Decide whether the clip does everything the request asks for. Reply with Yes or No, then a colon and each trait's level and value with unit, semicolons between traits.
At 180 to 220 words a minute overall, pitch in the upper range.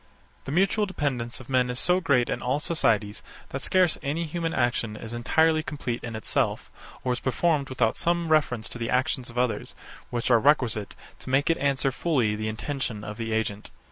No: average, 195 wpm; low, 130 Hz